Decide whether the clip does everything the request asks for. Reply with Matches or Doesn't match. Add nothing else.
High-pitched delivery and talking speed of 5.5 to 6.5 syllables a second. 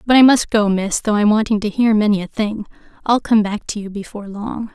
Matches